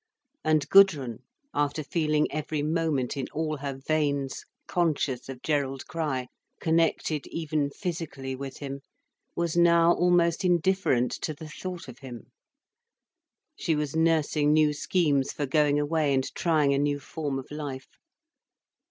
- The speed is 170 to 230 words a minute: No, slow, 135 wpm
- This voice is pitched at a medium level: Yes, medium, 150 Hz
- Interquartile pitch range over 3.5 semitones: No, average, 2.8 semitones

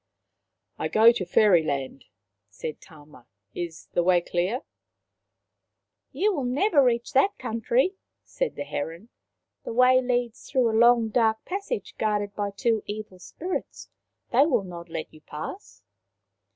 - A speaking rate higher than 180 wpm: No, average, 155 wpm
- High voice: Yes, high, 220 Hz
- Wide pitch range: Yes, wide, 6.4 semitones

